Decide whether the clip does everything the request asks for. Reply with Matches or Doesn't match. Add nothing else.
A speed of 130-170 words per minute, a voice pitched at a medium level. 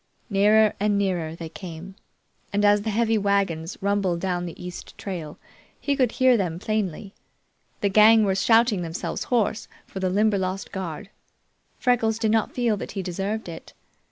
Doesn't match